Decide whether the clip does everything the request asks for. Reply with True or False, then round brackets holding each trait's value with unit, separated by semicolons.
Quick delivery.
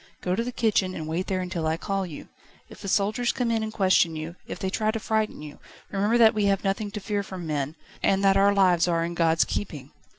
True (245 wpm)